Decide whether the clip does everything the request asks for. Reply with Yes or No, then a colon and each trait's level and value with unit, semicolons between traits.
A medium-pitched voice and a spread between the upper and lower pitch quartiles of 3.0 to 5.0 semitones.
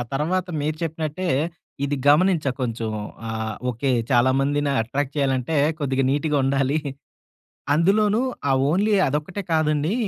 Yes: medium, 145 Hz; average, 3.5 semitones